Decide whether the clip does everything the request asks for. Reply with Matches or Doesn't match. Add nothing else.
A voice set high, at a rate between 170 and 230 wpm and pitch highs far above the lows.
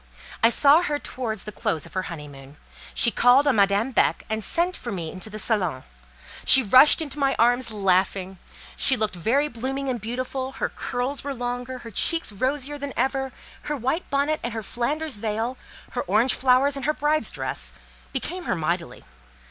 Doesn't match